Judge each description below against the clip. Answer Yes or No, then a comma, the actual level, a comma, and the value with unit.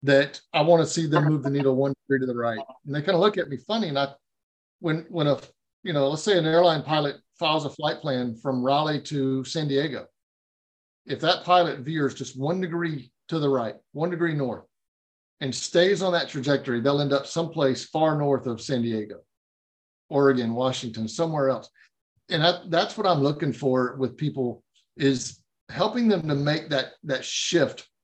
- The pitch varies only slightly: No, average, 3.7 semitones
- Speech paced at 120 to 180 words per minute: No, average, 195 wpm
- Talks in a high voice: No, medium, 140 Hz